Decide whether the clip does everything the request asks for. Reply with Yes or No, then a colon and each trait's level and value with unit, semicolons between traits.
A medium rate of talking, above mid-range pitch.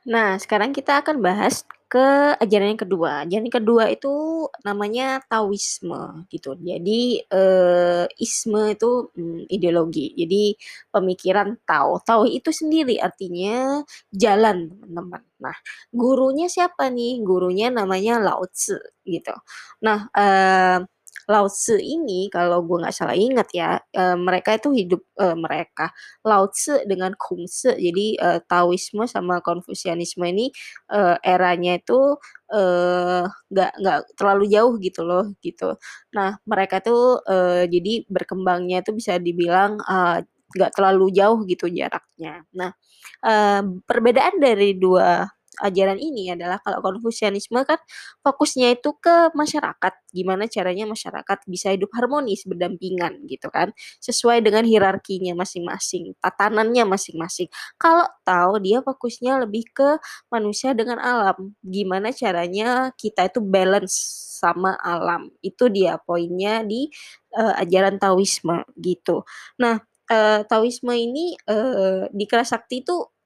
Yes: average, 125 wpm; high, 200 Hz